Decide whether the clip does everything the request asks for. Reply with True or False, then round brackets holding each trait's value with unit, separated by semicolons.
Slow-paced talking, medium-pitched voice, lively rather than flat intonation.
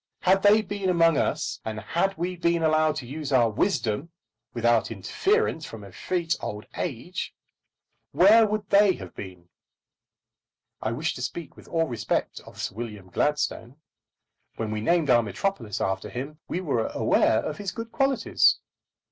False (155 wpm; 155 Hz; 8.5 semitones)